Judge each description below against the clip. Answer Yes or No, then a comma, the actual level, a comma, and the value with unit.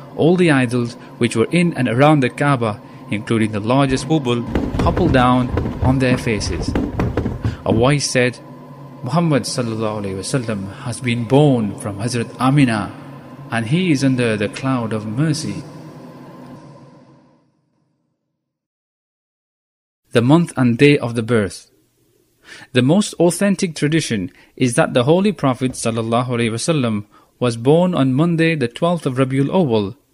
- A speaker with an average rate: No, slow, 130 wpm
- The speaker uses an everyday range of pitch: Yes, average, 3.8 semitones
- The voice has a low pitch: Yes, low, 130 Hz